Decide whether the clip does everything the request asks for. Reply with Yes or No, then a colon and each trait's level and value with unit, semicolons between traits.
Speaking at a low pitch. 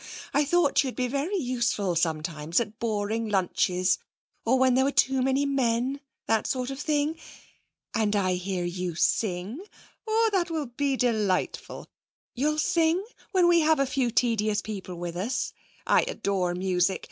No: high, 235 Hz